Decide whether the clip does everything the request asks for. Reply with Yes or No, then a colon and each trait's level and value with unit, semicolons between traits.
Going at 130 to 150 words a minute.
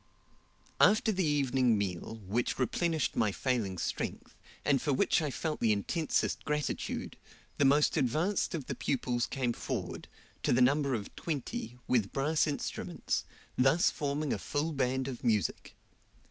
Yes: average, 145 wpm